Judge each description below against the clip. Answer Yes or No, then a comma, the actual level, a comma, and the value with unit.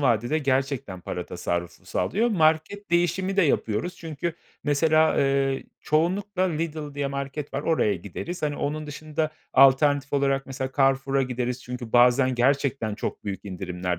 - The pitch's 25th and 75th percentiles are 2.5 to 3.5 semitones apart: No, average, 3.9 semitones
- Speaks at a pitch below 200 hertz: Yes, medium, 140 Hz